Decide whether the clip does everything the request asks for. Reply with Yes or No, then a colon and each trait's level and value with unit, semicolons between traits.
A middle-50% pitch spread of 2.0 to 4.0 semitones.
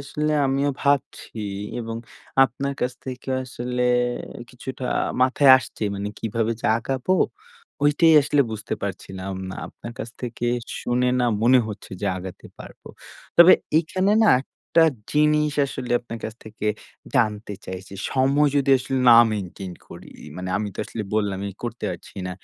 No: average, 4.8 semitones